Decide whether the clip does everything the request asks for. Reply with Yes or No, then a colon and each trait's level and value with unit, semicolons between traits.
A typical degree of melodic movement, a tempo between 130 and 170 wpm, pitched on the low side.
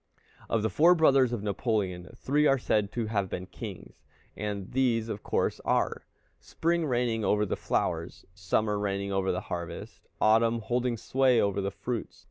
Yes: average, 3.9 semitones; average, 165 wpm; low, 110 Hz